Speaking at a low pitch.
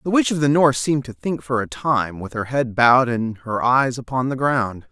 Yes: low, 125 Hz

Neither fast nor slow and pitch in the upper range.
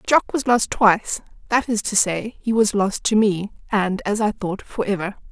No: fast, 215 wpm; high, 210 Hz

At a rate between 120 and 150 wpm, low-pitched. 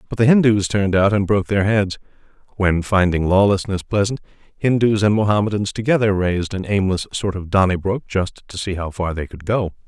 No: average, 190 wpm; low, 100 Hz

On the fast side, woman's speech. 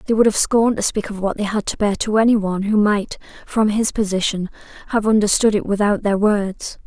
Yes: fast, 225 wpm; female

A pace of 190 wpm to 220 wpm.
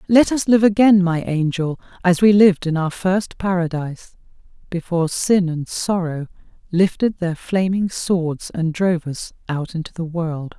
No: average, 160 wpm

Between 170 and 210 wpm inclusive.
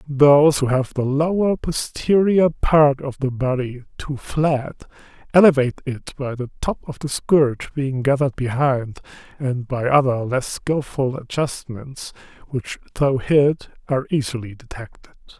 No: slow, 135 wpm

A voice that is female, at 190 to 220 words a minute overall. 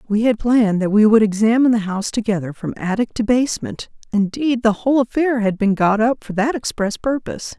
Yes: female; fast, 205 wpm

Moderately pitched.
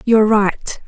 No: high, 215 Hz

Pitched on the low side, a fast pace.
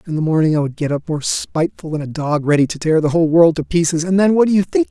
No: medium, 165 Hz; fast, 320 wpm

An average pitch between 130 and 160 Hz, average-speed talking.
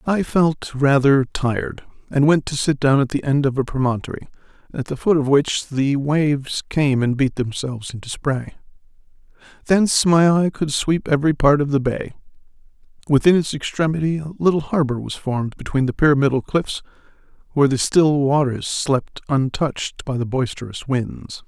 Yes: medium, 140 Hz; average, 170 wpm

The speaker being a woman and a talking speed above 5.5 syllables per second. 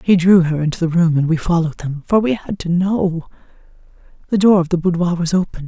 Yes: female; 6.0 syllables/s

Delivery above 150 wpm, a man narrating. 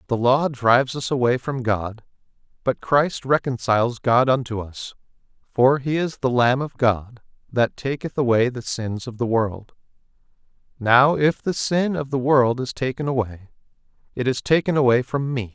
Yes: average, 170 wpm; male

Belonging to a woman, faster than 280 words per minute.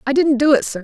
Yes: female; fast, 360 wpm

